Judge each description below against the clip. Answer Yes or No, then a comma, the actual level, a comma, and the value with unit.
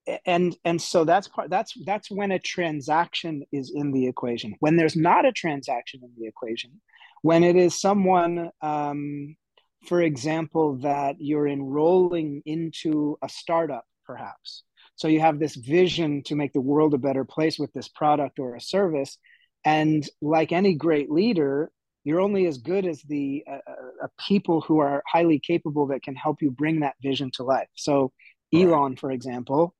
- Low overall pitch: No, medium, 155 Hz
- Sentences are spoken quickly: No, average, 170 wpm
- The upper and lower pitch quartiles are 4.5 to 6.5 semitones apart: No, average, 3.2 semitones